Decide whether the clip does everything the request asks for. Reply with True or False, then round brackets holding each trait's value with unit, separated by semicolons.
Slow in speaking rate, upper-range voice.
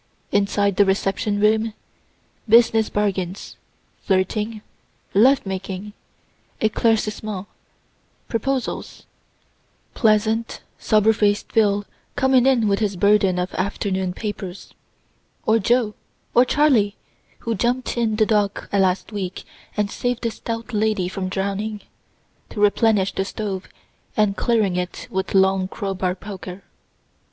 True (115 wpm; 210 Hz)